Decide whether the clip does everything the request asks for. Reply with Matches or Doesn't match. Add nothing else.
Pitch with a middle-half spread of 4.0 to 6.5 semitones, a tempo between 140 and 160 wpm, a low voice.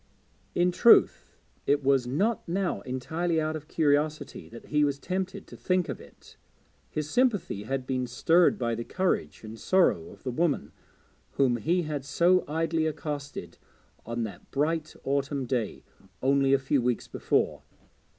Doesn't match